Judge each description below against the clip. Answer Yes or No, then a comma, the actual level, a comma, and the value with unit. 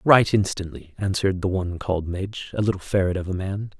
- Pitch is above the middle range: No, very low, 95 Hz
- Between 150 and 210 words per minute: Yes, fast, 205 wpm